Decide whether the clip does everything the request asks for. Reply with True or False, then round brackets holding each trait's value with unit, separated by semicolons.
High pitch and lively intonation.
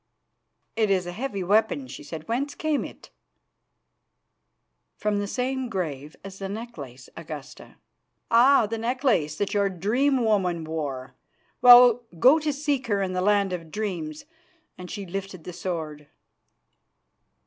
True (200 Hz; 6.2 semitones)